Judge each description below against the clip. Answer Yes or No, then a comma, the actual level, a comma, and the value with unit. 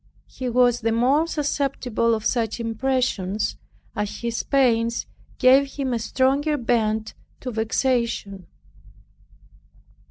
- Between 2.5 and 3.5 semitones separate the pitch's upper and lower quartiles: Yes, average, 2.9 semitones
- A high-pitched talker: Yes, high, 240 Hz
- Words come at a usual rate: No, slow, 105 wpm